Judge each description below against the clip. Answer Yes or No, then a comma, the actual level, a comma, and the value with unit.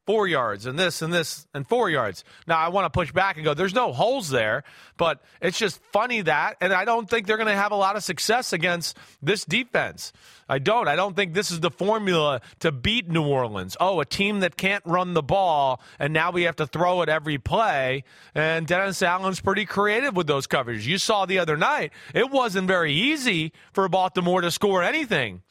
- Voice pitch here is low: No, medium, 180 Hz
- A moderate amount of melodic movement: Yes, average, 4.0 semitones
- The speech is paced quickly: Yes, fast, 215 wpm